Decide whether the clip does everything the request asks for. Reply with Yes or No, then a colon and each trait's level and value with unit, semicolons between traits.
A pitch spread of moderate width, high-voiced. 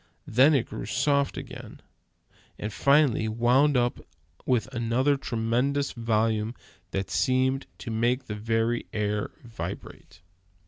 No: average, 3.0 semitones; low, 120 Hz